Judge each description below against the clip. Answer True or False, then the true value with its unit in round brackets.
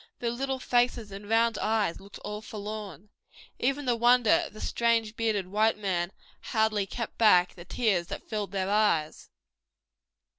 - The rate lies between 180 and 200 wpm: False (155 wpm)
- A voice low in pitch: False (215 Hz)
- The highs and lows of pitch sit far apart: False (2.7 semitones)